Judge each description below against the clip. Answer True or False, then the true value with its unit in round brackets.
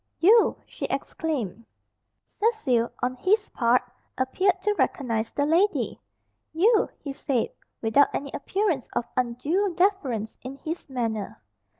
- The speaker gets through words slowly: True (120 wpm)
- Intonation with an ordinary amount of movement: False (7.9 semitones)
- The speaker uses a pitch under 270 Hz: False (280 Hz)